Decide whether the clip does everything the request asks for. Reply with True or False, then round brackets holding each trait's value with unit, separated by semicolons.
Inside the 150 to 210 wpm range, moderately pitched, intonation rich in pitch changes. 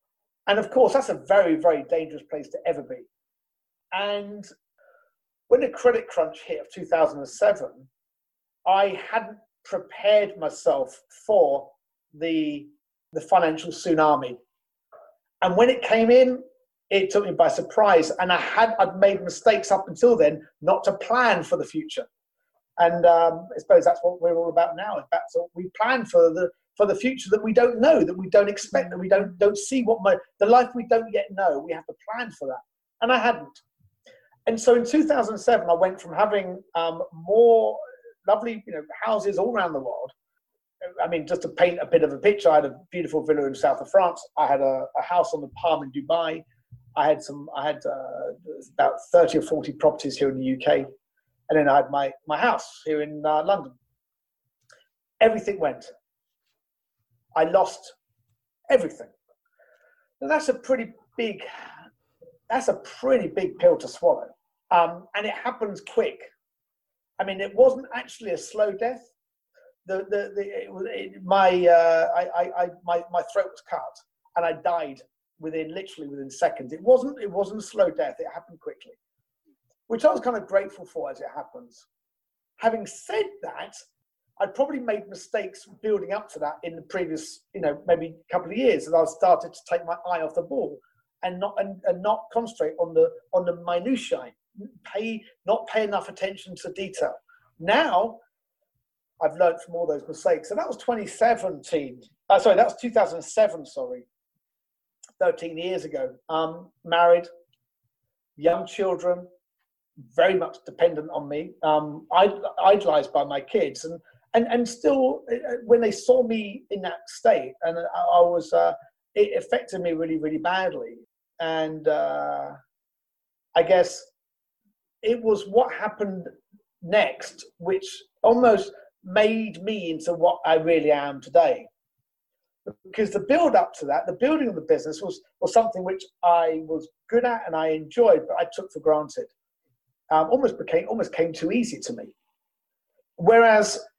False (170 wpm; 200 Hz; 7.2 semitones)